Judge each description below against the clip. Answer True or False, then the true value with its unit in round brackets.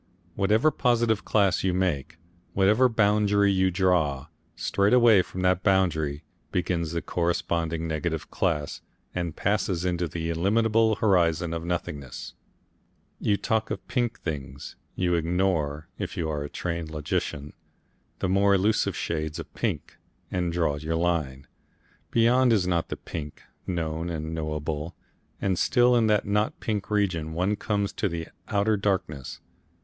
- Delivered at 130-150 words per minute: True (145 wpm)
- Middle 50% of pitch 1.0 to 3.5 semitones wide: False (4.1 semitones)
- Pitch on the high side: False (90 Hz)